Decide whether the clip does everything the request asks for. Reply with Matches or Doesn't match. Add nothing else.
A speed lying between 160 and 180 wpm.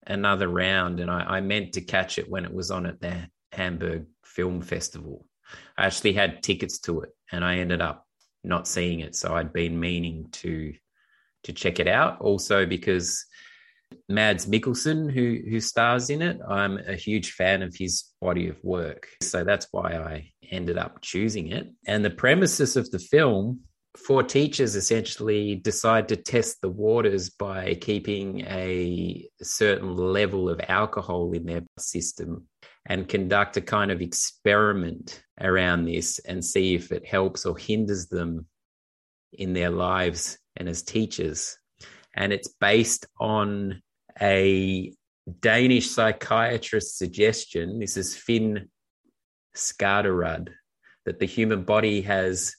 Doesn't match